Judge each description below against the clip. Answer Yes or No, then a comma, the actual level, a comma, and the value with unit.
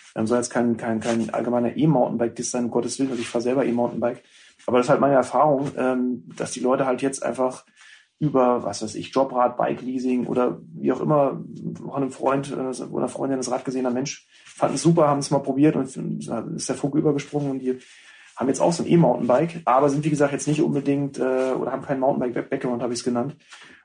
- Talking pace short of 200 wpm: No, fast, 215 wpm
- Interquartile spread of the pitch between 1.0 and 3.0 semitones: Yes, narrow, 2.5 semitones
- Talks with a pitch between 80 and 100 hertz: No, low, 130 Hz